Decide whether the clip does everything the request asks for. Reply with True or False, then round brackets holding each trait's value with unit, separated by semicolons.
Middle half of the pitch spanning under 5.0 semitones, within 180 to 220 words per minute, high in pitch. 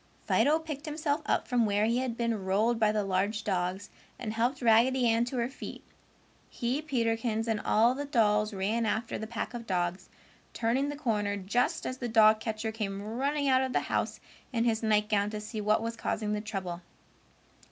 True (2.8 semitones; 195 wpm; 225 Hz)